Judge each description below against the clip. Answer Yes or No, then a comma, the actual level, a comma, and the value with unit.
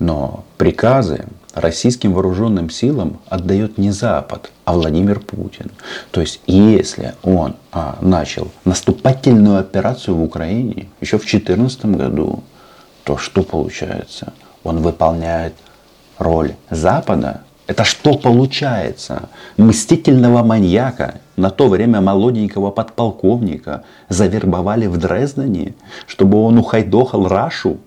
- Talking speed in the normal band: No, slow, 105 wpm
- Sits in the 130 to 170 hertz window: No, low, 100 Hz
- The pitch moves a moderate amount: Yes, average, 4.5 semitones